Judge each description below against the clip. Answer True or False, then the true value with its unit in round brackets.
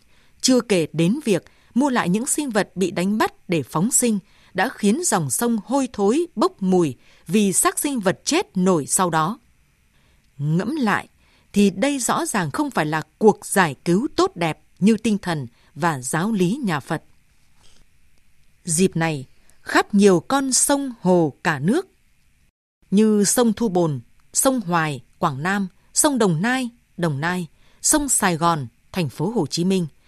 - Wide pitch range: True (5.9 semitones)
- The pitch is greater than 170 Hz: True (190 Hz)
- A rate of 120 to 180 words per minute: True (165 wpm)